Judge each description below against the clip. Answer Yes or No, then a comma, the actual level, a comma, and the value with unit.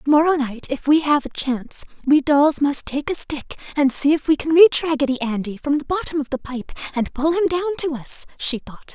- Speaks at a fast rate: Yes, fast, 235 wpm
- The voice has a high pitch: Yes, very high, 290 Hz